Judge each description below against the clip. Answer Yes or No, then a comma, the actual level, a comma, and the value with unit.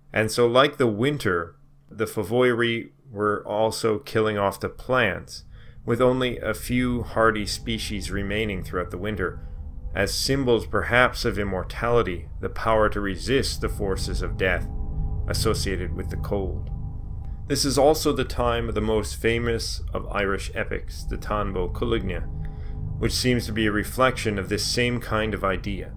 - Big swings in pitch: No, average, 4.2 semitones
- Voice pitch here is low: Yes, low, 105 Hz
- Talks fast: No, average, 155 wpm